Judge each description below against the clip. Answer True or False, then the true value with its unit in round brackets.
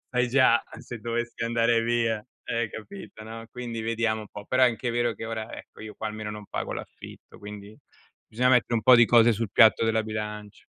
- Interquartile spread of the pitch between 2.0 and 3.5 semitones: False (1.6 semitones)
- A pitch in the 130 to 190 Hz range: False (115 Hz)